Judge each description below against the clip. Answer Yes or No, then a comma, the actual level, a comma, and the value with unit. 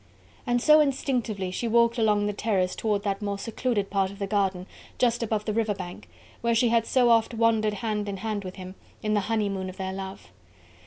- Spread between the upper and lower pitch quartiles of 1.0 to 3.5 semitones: Yes, average, 2.7 semitones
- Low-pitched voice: No, high, 210 Hz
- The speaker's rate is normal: No, fast, 210 wpm